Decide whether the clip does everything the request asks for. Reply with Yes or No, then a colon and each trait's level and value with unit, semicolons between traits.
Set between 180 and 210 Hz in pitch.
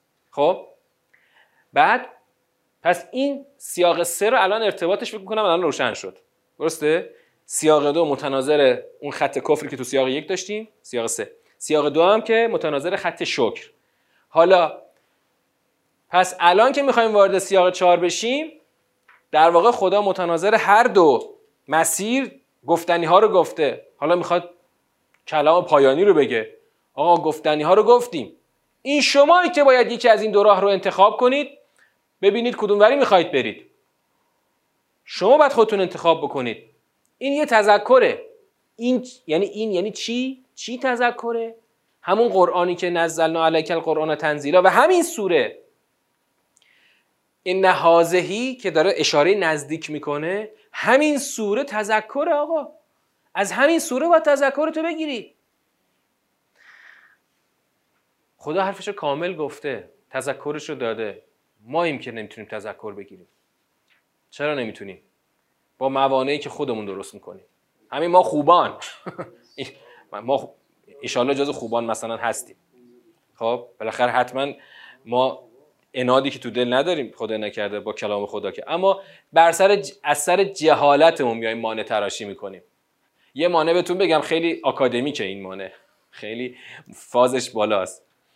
Yes: medium, 185 Hz